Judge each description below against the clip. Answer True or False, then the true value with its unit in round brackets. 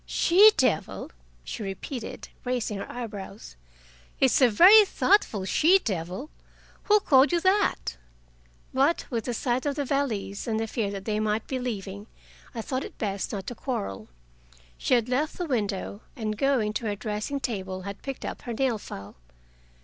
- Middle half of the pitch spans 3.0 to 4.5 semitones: False (5.1 semitones)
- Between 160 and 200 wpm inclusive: True (170 wpm)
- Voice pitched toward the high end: True (230 Hz)